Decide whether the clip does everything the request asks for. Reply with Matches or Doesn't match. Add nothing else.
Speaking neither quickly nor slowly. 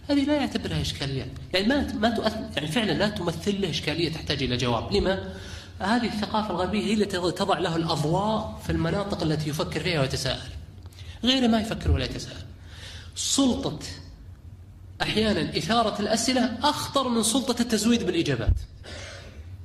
Doesn't match